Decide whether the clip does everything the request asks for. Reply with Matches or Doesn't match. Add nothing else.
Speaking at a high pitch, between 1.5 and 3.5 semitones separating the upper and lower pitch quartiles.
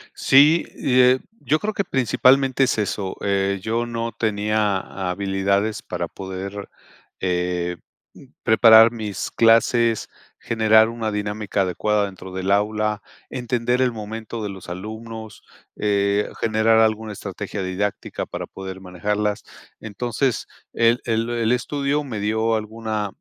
Doesn't match